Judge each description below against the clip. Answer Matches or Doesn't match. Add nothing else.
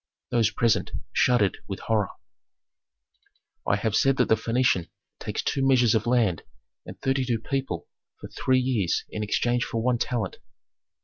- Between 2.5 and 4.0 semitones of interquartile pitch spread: Matches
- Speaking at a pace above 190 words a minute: Doesn't match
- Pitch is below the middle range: Matches